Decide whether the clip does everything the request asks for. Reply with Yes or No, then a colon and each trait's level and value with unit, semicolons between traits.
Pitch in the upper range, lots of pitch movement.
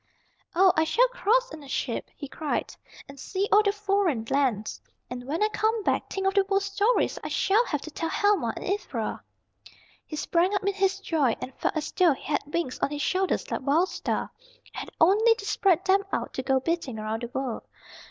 Yes: very high, 360 Hz; wide, 6.1 semitones